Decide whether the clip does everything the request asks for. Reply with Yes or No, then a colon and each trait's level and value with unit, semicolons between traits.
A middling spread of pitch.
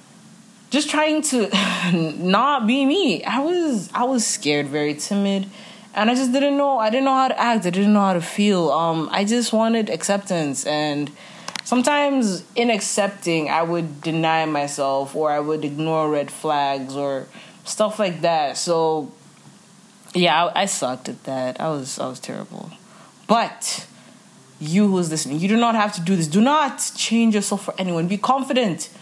No: wide, 6.3 semitones